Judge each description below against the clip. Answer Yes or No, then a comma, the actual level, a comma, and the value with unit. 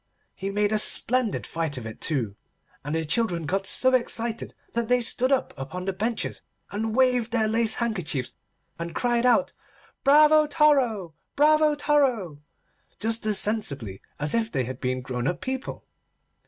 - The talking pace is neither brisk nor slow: Yes, average, 160 wpm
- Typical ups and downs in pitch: No, wide, 7.5 semitones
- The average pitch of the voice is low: No, high, 220 Hz